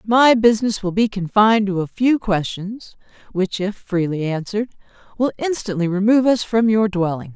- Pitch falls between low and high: No, high, 205 Hz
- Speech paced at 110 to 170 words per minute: Yes, average, 165 wpm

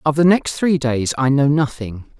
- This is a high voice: No, medium, 140 Hz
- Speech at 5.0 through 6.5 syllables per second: No, 4.5 syllables/s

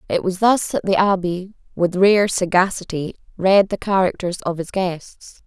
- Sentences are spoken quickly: No, average, 165 wpm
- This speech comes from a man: No, female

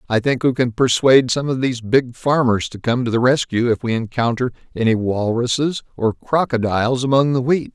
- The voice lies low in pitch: Yes, low, 125 Hz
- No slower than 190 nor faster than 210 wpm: Yes, average, 195 wpm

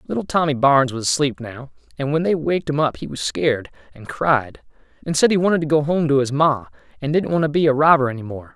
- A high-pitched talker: No, medium, 140 Hz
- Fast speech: Yes, fast, 250 wpm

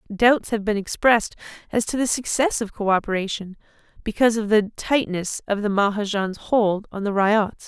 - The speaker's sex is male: No, female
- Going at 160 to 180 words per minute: Yes, average, 165 wpm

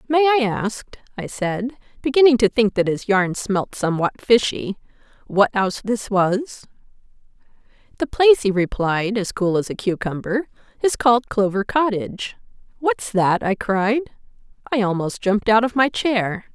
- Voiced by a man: No, female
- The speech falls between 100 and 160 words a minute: Yes, average, 150 wpm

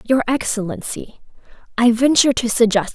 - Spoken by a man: No, female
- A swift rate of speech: No, slow, 120 wpm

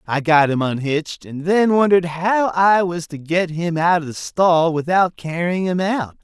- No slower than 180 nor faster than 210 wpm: Yes, average, 200 wpm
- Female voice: No, male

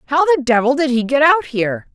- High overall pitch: Yes, very high, 260 Hz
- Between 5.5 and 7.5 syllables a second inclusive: Yes, 5.9 syllables/s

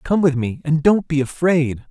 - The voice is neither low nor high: Yes, medium, 150 Hz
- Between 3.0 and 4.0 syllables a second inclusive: No, 4.6 syllables/s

